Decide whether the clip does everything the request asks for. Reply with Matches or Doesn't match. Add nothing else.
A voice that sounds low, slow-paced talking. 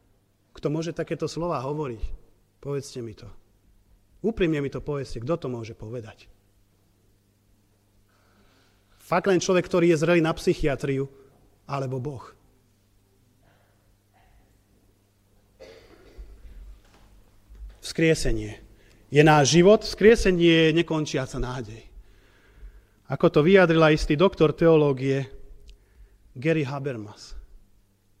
Matches